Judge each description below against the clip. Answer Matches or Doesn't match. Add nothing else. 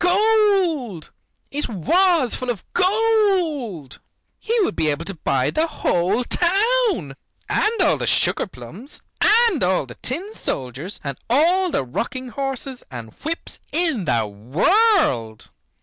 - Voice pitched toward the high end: Matches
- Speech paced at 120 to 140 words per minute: Matches